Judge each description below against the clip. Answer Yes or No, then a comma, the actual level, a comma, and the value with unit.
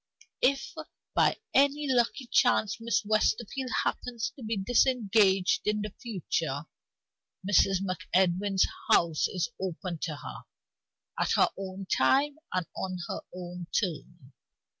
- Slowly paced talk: Yes, slow, 120 wpm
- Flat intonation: No, average, 4.7 semitones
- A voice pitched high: Yes, high, 195 Hz